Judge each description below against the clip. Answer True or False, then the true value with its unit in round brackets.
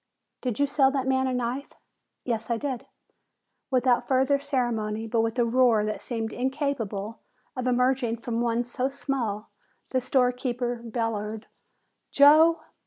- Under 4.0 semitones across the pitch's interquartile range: True (2.6 semitones)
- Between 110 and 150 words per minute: True (140 wpm)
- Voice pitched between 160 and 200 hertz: False (245 Hz)